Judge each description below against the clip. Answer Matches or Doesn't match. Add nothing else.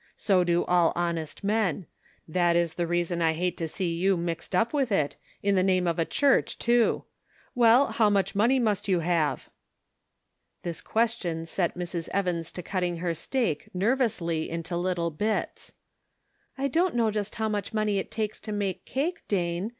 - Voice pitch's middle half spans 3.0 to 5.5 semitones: Matches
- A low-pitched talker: Doesn't match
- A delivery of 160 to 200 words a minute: Matches